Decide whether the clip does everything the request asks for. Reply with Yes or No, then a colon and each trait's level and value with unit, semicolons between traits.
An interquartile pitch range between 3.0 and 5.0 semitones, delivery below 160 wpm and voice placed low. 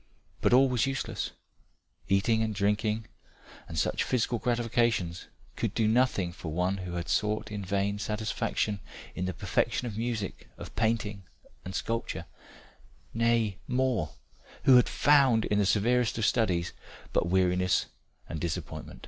Yes: average, 3.8 semitones; average, 140 wpm; low, 105 Hz